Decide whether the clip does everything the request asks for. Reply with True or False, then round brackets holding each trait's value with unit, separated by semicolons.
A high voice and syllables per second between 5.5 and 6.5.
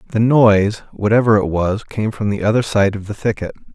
False (105 Hz; 5.7 syllables/s)